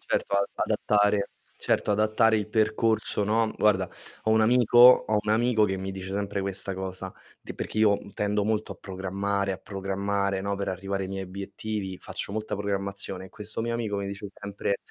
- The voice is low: Yes, low, 100 Hz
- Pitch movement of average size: No, narrow, 1.7 semitones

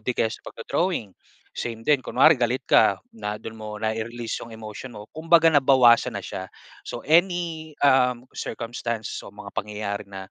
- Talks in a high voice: No, low, 115 Hz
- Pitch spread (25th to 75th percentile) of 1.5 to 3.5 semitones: No, average, 4.5 semitones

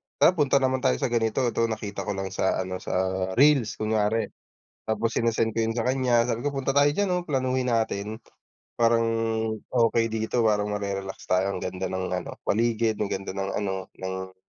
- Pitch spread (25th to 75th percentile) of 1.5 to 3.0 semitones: No, average, 3.8 semitones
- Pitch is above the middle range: No, low, 110 Hz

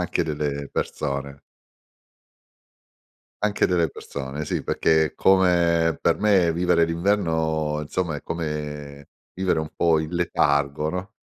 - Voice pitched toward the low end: Yes, very low, 80 Hz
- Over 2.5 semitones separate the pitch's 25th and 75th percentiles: Yes, average, 2.9 semitones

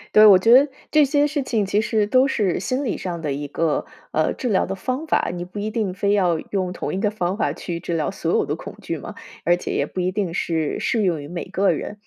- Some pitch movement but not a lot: Yes, average, 4.2 semitones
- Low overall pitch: No, high, 195 Hz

